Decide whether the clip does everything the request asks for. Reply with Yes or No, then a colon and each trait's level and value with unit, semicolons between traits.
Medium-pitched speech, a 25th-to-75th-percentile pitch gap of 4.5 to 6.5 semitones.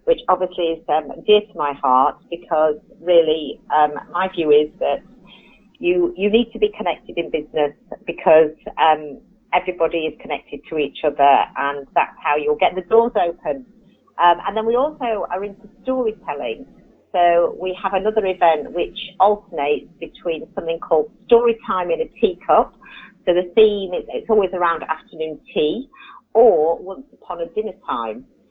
Yes: medium, 180 Hz; wide, 5.6 semitones